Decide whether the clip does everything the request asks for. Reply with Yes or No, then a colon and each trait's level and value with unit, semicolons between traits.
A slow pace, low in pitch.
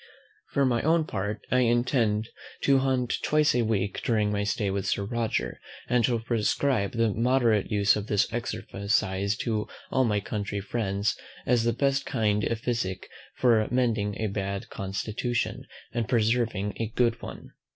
No: average, 160 wpm; low, 110 Hz